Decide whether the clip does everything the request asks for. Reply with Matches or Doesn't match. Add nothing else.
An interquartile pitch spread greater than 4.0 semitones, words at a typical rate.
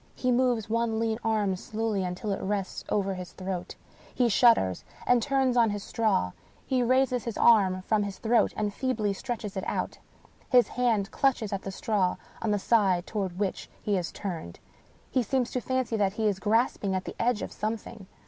Doesn't match